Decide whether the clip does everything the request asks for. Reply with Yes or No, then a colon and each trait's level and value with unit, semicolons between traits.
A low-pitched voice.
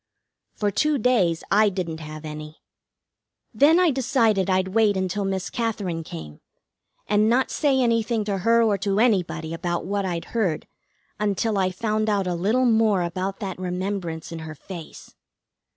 No: high, 195 Hz